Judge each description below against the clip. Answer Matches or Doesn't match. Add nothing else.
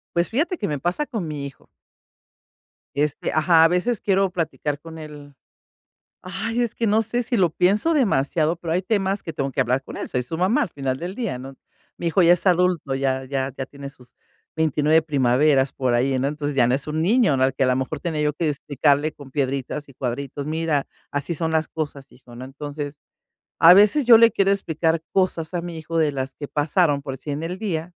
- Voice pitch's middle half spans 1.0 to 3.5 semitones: Doesn't match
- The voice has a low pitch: Doesn't match